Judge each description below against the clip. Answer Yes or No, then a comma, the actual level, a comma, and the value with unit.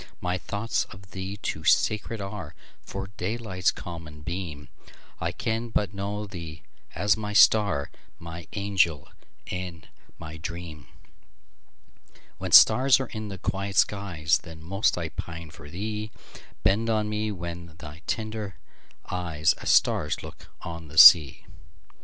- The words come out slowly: Yes, slow, 115 wpm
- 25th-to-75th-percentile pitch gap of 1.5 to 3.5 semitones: No, average, 4.2 semitones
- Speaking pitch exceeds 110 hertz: No, very low, 90 Hz